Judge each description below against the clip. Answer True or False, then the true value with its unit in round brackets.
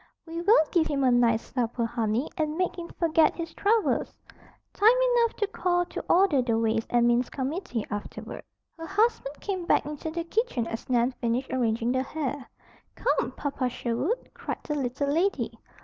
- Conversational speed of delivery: True (175 wpm)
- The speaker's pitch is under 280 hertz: False (290 Hz)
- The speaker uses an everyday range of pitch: False (6.6 semitones)